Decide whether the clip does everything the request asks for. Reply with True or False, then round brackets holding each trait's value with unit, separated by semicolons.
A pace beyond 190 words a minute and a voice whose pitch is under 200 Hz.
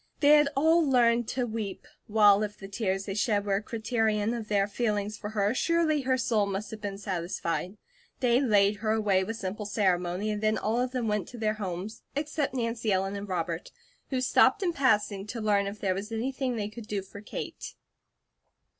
False (200 wpm; 215 Hz)